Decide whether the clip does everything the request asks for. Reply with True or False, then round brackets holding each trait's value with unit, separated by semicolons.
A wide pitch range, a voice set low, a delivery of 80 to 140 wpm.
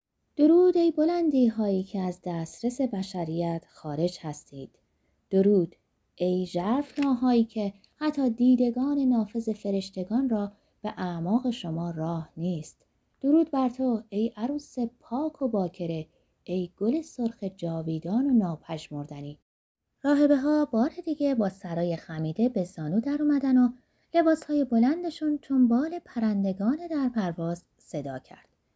False (7.4 semitones; 225 Hz; 130 wpm)